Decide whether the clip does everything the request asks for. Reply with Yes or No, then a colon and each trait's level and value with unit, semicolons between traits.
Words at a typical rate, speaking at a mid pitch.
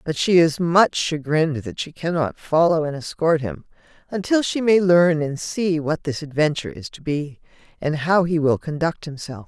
Yes: average, 190 wpm; medium, 160 Hz